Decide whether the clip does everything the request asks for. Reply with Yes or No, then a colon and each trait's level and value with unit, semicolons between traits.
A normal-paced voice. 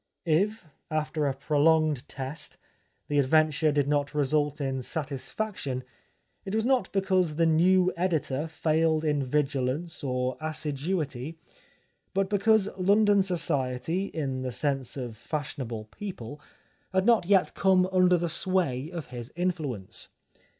No: slow, 130 wpm